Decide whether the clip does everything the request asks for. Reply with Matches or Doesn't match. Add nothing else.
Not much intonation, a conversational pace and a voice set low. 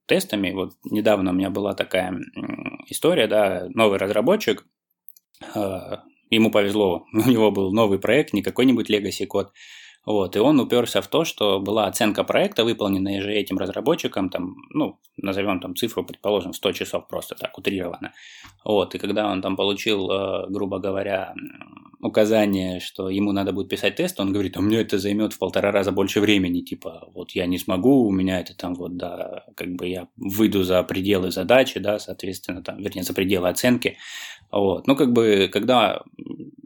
Doesn't match